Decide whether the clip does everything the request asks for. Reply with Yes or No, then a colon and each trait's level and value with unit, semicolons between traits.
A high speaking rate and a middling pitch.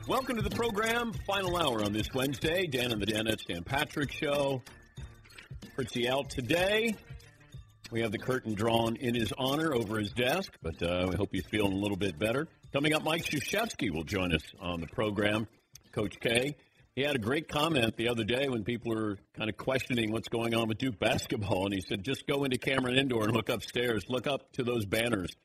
No: fast, 210 wpm; low, 120 Hz